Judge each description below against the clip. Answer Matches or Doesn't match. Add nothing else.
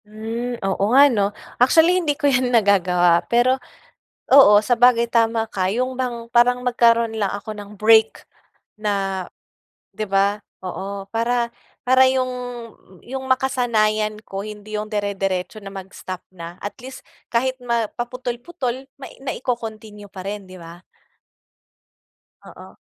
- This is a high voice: Matches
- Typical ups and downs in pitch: Matches